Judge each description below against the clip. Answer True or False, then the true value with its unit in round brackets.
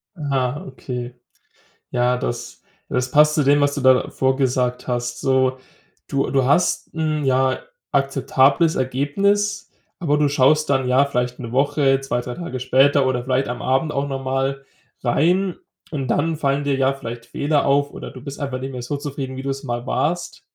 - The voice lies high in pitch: False (135 Hz)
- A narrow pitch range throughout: True (2.1 semitones)